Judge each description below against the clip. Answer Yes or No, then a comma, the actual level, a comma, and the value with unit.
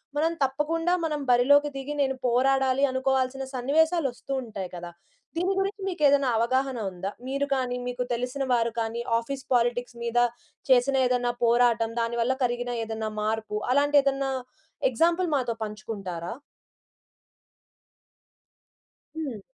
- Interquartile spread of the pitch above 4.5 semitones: No, average, 3.0 semitones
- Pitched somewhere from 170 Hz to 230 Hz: No, very high, 255 Hz